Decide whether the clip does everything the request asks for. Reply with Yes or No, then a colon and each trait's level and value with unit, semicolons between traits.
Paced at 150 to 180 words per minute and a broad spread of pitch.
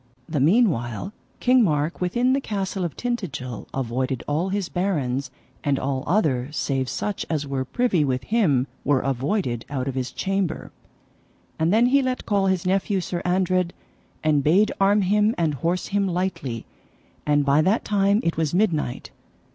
Yes: average, 165 wpm; wide, 6.3 semitones